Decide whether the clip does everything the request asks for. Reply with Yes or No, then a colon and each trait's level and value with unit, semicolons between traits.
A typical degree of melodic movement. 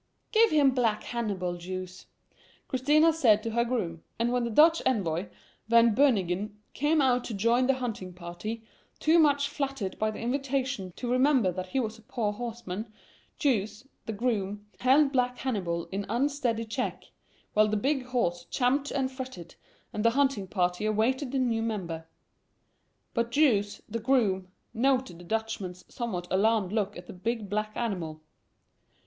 Yes: average, 4.8 semitones